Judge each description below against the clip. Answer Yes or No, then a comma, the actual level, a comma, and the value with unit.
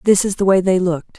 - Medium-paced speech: No, fast, 305 wpm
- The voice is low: No, medium, 185 Hz